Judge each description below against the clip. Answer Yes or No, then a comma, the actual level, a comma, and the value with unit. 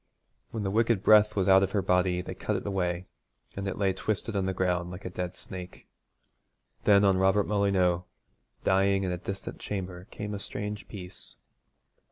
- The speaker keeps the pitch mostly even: Yes, narrow, 1.9 semitones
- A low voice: Yes, very low, 95 Hz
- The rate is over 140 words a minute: Yes, average, 185 wpm